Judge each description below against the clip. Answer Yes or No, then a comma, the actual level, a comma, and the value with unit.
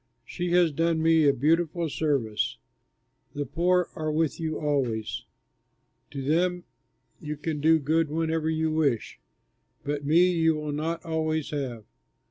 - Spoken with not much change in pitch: Yes, narrow, 2.1 semitones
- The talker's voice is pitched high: No, medium, 155 Hz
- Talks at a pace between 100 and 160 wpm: Yes, average, 140 wpm